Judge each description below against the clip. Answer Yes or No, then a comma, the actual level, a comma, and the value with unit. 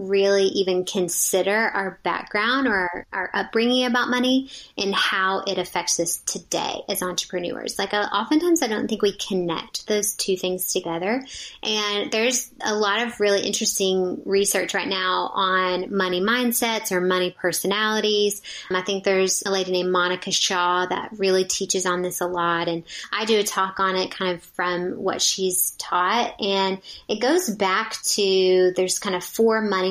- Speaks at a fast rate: No, average, 170 wpm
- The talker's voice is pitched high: Yes, high, 195 Hz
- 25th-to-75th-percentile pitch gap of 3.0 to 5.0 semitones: No, narrow, 2.4 semitones